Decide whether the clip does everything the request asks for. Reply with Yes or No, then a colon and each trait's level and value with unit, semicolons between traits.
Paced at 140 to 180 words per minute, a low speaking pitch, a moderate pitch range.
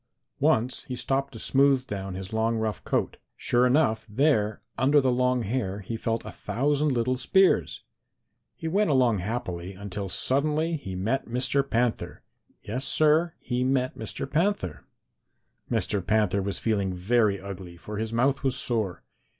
Yes: average, 155 wpm; low, 120 Hz; average, 4.9 semitones